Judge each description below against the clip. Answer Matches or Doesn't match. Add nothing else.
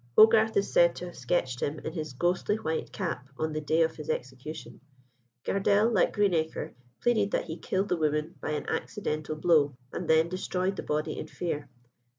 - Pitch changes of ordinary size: Matches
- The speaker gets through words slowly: Doesn't match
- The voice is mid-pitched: Matches